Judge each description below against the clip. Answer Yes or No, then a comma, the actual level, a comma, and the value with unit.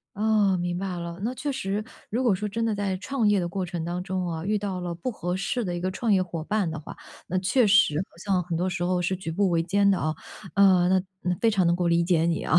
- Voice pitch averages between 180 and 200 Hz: Yes, medium, 185 Hz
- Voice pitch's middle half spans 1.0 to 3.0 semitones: Yes, average, 2.7 semitones